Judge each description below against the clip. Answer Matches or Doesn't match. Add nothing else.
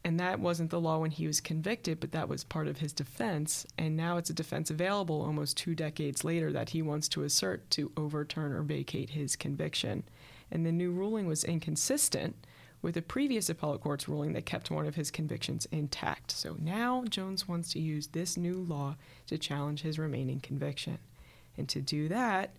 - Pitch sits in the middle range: Matches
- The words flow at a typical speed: Matches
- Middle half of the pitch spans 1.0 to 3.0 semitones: Matches